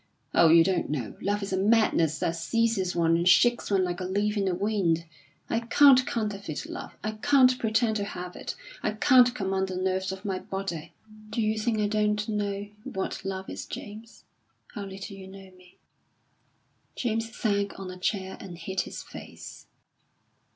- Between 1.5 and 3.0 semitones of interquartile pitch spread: Yes, average, 2.7 semitones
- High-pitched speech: Yes, high, 195 Hz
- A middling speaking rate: Yes, average, 180 wpm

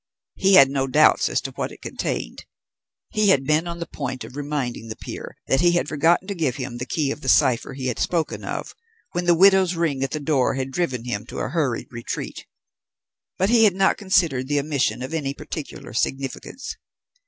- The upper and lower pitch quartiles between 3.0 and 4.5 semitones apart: No, average, 4.9 semitones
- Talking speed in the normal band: No, fast, 210 wpm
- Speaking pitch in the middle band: Yes, medium, 145 Hz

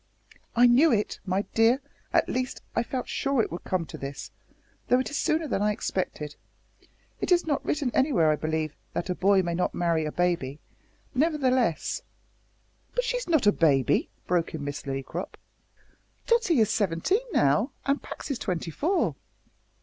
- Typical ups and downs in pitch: No, wide, 9.0 semitones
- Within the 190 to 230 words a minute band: No, average, 175 wpm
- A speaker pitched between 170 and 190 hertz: No, high, 210 Hz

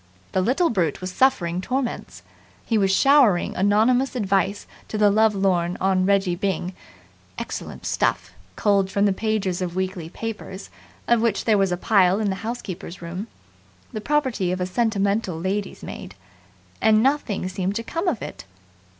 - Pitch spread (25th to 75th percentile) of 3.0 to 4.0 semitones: Yes, average, 3.3 semitones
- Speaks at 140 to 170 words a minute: Yes, average, 160 wpm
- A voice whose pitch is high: Yes, high, 200 Hz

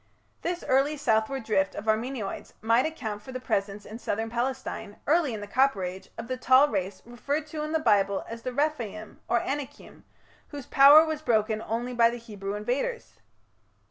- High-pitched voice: Yes, high, 235 Hz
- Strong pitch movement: No, average, 4.5 semitones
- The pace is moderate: Yes, average, 180 wpm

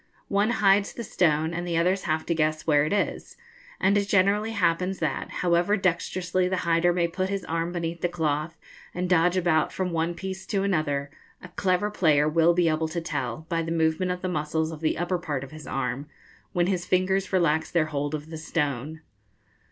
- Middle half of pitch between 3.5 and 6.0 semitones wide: No, average, 2.8 semitones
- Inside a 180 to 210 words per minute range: Yes, fast, 205 wpm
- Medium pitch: Yes, medium, 170 Hz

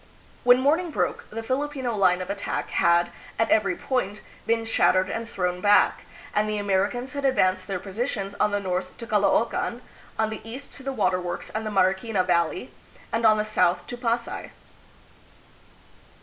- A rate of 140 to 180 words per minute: Yes, average, 170 wpm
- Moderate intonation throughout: Yes, average, 4.2 semitones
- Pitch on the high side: Yes, high, 215 Hz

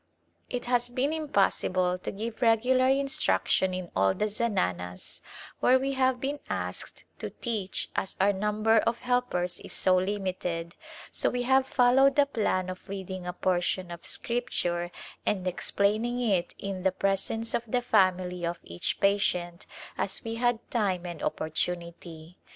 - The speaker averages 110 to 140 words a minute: No, average, 155 wpm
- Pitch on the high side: Yes, high, 200 Hz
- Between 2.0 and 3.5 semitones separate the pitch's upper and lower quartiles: No, average, 5.2 semitones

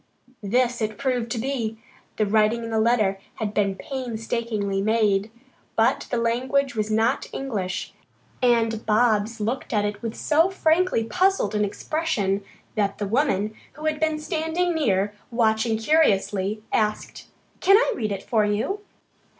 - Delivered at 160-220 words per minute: No, average, 150 wpm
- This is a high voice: Yes, high, 225 Hz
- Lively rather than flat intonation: No, average, 4.4 semitones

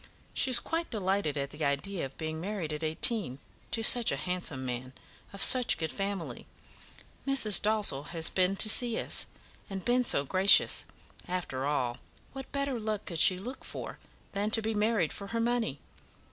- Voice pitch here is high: Yes, high, 195 Hz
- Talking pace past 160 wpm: Yes, average, 180 wpm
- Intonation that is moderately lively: No, wide, 6.3 semitones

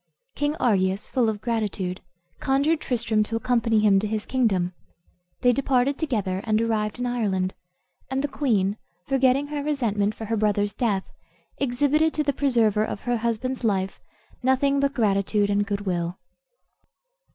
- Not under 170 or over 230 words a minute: No, average, 150 wpm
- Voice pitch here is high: Yes, high, 225 Hz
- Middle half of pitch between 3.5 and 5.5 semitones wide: Yes, average, 4.4 semitones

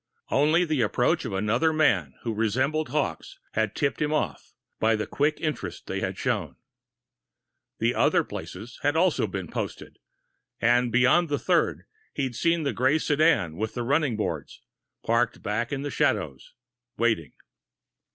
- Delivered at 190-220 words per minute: No, average, 150 wpm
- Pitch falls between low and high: No, low, 125 Hz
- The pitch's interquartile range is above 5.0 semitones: Yes, wide, 5.5 semitones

